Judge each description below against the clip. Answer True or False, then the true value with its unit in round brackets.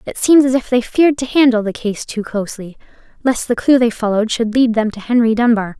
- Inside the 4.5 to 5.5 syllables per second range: False (6.0 syllables/s)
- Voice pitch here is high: True (235 Hz)